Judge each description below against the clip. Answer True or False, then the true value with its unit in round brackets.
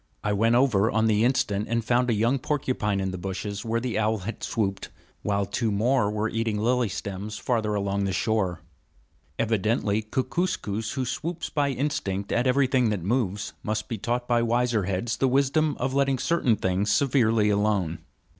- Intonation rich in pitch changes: False (3.6 semitones)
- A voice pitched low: True (110 Hz)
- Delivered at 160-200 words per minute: True (175 wpm)